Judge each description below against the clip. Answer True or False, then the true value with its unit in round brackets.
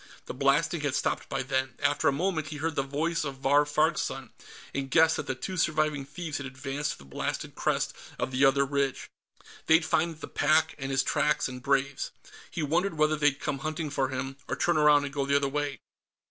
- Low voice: False (145 Hz)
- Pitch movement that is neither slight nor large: False (2.3 semitones)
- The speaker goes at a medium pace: False (215 wpm)